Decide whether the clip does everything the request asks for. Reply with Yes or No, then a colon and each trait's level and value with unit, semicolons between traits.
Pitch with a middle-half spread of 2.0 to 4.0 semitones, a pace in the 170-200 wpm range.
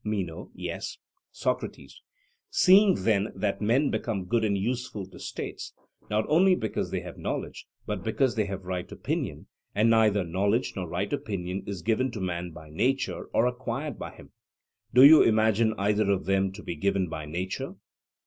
Yes: average, 3.5 semitones; average, 175 wpm